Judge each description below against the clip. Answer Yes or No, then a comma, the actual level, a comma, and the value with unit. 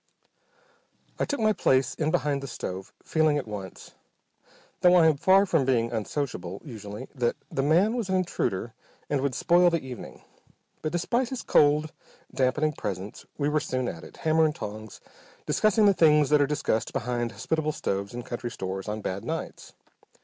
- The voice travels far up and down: Yes, wide, 6.0 semitones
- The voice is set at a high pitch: No, medium, 140 Hz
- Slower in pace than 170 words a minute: No, average, 175 wpm